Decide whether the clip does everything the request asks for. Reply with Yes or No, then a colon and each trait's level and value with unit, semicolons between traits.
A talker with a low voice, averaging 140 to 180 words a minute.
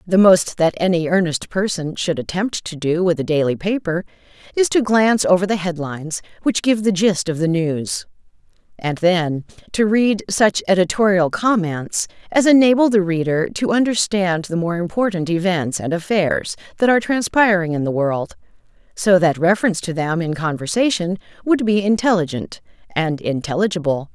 No: medium, 180 Hz; average, 160 wpm